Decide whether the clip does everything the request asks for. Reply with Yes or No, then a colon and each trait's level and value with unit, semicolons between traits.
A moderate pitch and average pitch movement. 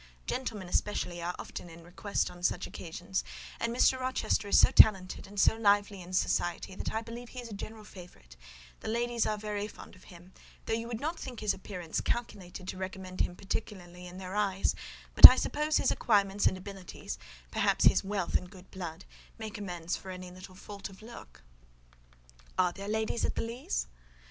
No: high, 195 Hz; average, 3.3 semitones